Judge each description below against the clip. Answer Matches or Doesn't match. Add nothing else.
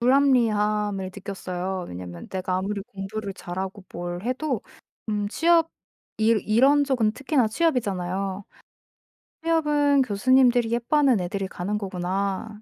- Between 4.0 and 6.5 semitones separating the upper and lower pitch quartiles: Matches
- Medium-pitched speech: Doesn't match